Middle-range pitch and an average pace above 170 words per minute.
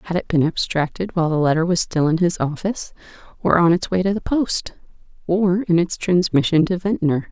Yes: medium, 175 Hz; average, 190 wpm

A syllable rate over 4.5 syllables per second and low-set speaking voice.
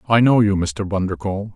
Yes: 5.8 syllables/s; low, 100 Hz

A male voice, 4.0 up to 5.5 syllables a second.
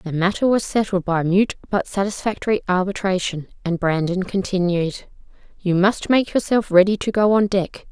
No: female; 5.0 syllables/s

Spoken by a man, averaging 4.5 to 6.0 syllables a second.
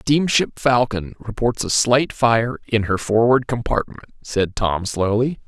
No: male; 4.1 syllables/s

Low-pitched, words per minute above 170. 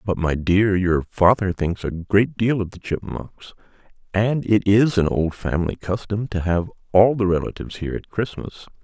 Yes: very low, 95 Hz; average, 185 wpm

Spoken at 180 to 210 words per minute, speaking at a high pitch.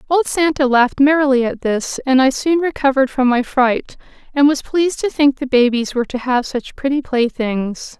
Yes: average, 195 wpm; very high, 265 Hz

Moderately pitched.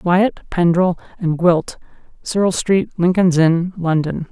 Yes: medium, 175 Hz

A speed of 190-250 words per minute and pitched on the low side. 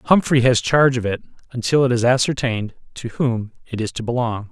Yes: average, 200 wpm; low, 120 Hz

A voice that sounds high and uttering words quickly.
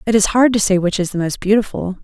Yes: high, 200 Hz; fast, 295 wpm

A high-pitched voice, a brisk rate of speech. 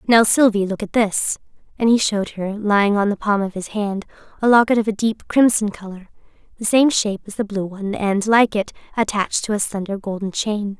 Yes: high, 210 Hz; fast, 215 wpm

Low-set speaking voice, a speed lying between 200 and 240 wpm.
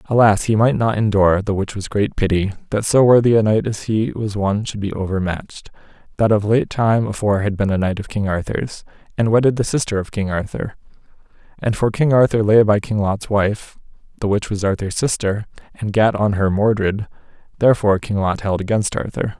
Yes: low, 105 Hz; fast, 205 wpm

